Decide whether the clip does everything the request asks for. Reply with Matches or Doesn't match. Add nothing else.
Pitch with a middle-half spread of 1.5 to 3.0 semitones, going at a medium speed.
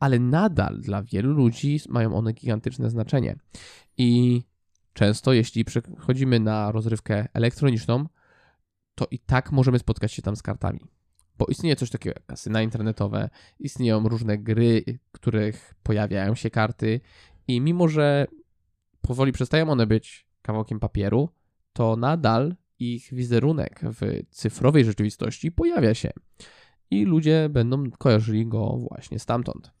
Doesn't match